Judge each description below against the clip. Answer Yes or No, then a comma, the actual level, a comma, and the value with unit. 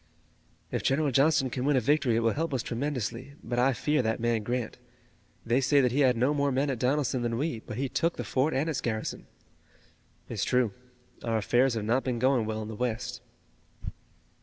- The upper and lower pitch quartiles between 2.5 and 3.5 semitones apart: Yes, average, 3.1 semitones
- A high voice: No, low, 125 Hz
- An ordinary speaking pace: No, fast, 210 wpm